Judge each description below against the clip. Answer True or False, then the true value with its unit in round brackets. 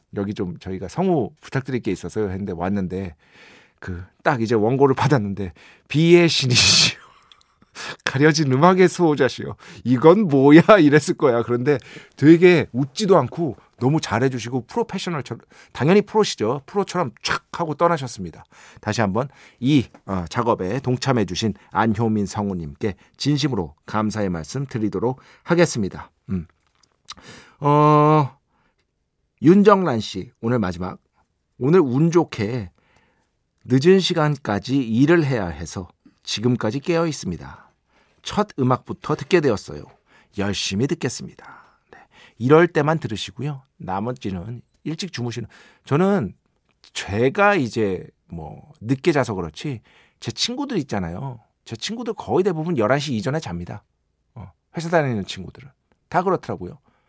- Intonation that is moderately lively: False (7.8 semitones)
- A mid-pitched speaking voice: False (130 Hz)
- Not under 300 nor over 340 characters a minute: False (285 characters per minute)